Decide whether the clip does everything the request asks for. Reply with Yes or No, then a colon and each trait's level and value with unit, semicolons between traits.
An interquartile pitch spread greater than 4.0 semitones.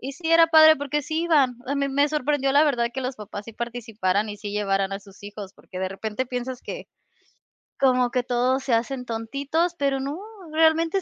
Yes: average, 4.7 semitones